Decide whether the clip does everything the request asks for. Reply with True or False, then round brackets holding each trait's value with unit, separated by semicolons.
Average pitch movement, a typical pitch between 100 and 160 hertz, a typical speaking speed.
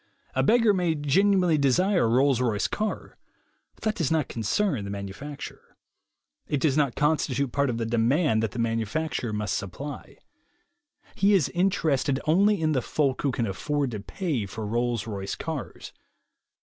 False (6.0 semitones; 140 Hz; 170 wpm)